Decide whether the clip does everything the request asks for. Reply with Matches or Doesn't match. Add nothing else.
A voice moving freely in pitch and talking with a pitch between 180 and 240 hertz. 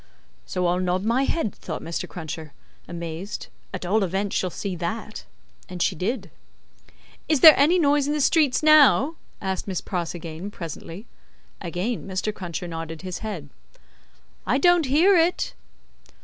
Matches